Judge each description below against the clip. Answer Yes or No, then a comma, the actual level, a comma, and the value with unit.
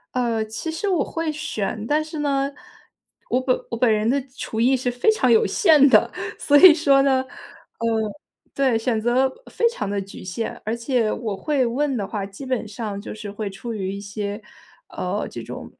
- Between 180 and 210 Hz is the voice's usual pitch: No, high, 240 Hz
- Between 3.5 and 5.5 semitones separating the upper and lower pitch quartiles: Yes, average, 4.6 semitones